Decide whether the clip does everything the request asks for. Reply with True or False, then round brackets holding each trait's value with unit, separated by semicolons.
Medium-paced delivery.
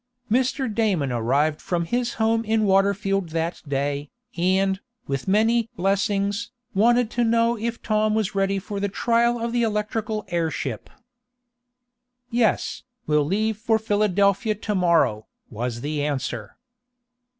False (130 wpm)